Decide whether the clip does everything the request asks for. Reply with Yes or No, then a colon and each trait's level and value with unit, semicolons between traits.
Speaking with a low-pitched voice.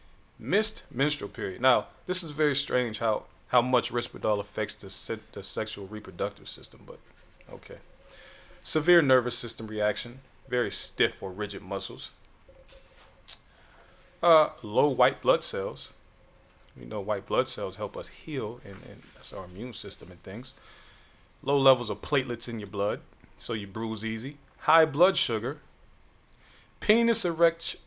Yes: low, 120 Hz